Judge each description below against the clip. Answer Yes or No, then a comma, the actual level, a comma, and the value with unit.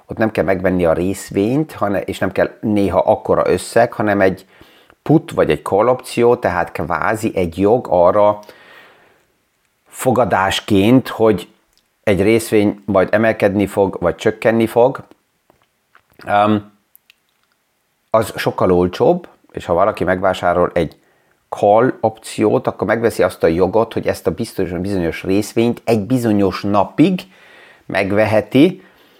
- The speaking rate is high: No, average, 125 wpm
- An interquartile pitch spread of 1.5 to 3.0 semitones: Yes, narrow, 2.6 semitones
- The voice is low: Yes, low, 105 Hz